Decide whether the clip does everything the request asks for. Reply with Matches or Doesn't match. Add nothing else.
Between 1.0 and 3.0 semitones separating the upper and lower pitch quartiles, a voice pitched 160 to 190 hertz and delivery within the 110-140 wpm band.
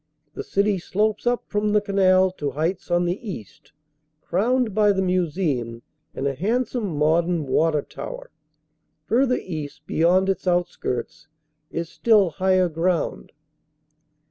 Doesn't match